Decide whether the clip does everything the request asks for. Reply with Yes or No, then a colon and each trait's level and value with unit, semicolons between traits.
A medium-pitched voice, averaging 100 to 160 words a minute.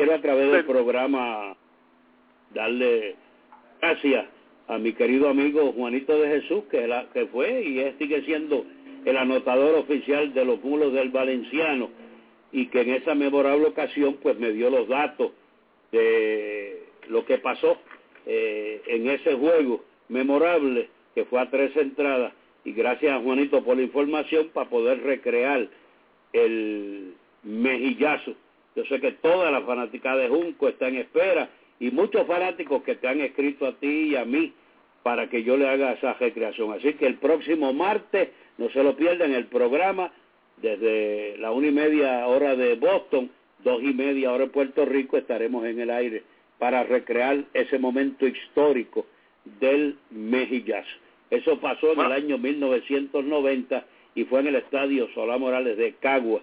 Yes: medium, 145 Hz; average, 155 wpm